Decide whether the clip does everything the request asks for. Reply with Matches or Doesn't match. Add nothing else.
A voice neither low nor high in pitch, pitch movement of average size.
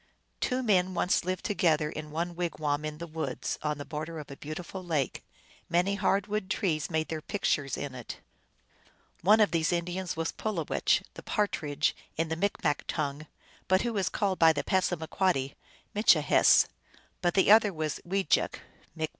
Matches